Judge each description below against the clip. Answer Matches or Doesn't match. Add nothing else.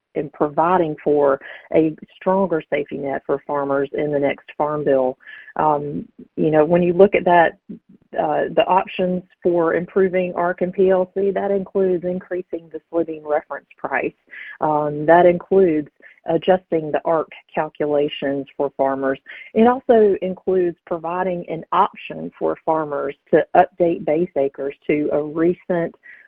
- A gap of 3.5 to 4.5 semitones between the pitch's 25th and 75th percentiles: Matches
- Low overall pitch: Doesn't match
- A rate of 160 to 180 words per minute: Doesn't match